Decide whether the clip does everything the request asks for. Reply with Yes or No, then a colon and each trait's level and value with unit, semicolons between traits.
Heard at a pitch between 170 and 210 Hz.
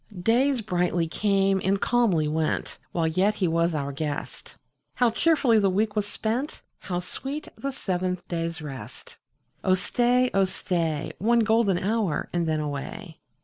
Yes: high, 190 Hz